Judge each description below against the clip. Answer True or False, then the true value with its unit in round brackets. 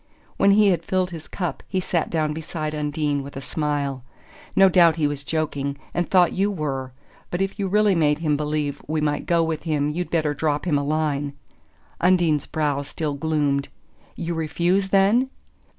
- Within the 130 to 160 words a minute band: False (180 wpm)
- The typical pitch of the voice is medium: True (155 Hz)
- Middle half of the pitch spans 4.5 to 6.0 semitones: False (3.3 semitones)